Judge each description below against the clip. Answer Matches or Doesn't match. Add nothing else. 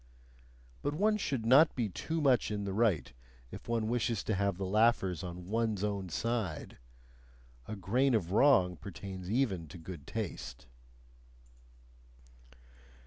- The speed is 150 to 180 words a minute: Doesn't match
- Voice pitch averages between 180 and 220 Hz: Doesn't match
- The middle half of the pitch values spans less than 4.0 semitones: Doesn't match